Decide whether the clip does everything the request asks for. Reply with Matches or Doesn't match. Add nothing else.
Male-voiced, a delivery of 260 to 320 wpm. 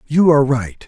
Doesn't match